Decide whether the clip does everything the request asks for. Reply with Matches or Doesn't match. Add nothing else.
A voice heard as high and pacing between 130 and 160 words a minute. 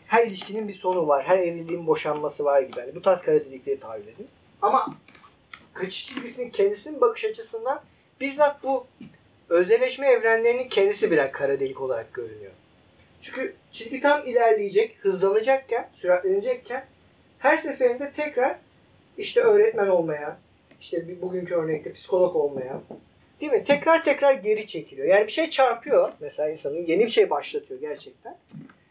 Matches